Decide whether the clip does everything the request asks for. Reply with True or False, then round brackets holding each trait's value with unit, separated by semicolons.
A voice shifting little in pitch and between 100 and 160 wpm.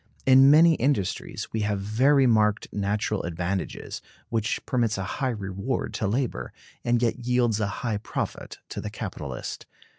False (3.8 semitones; 150 wpm)